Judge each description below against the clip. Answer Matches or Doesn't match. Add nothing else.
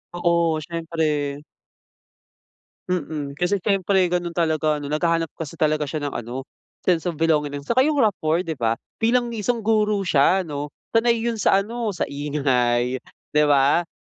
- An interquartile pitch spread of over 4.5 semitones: Matches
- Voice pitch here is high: Doesn't match